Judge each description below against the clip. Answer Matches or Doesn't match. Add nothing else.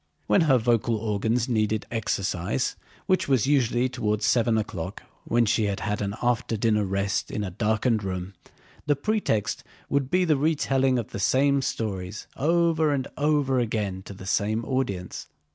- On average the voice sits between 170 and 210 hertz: Doesn't match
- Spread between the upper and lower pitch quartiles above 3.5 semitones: Matches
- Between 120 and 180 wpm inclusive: Matches